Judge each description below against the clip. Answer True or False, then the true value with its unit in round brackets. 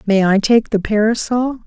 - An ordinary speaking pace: True (180 wpm)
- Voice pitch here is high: True (220 Hz)